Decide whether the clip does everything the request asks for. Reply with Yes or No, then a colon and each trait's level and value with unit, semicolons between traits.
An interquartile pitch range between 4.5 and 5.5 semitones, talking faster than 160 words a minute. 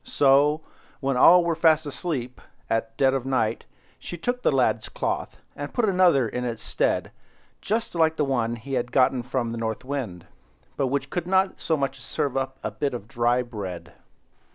Yes: average, 4.9 semitones; average, 185 wpm